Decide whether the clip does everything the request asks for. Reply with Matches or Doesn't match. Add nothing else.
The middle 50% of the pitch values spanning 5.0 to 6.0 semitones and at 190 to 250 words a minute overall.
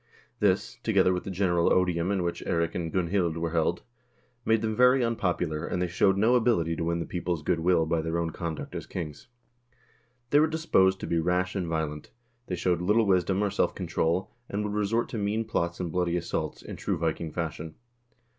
Doesn't match